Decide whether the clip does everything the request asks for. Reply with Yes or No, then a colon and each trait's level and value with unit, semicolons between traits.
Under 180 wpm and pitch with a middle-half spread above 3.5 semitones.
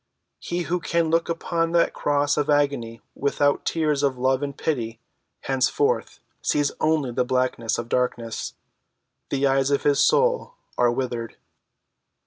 Yes: average, 140 wpm; average, 4.0 semitones